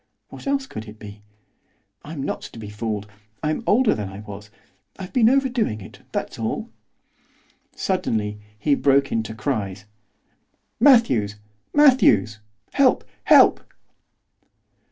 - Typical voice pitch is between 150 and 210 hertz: No, low, 115 Hz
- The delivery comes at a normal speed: No, slow, 120 wpm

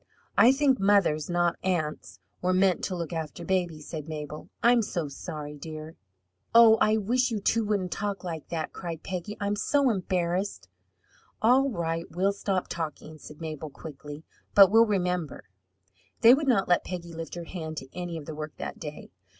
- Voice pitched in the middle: Yes, medium, 175 Hz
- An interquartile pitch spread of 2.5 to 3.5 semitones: No, average, 4.4 semitones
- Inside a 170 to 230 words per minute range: Yes, average, 175 wpm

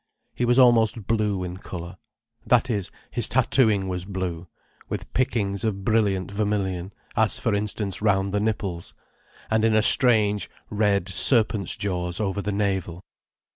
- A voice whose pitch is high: No, low, 100 Hz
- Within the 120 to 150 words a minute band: Yes, average, 140 wpm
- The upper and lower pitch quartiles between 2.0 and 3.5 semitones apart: Yes, average, 2.7 semitones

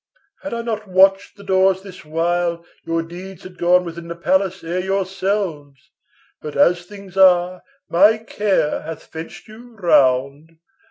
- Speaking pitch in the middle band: Yes, medium, 180 Hz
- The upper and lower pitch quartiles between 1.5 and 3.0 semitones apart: Yes, average, 2.7 semitones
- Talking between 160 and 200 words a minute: No, average, 150 wpm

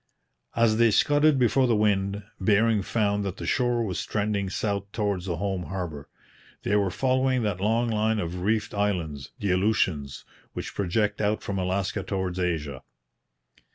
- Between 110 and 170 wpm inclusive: Yes, average, 155 wpm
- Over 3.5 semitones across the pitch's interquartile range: No, average, 3.0 semitones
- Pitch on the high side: No, low, 100 Hz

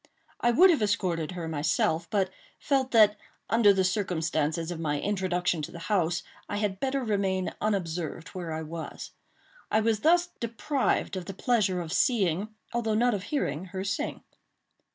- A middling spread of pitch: Yes, average, 4.5 semitones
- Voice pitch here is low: No, high, 190 Hz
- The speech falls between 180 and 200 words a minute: No, average, 165 wpm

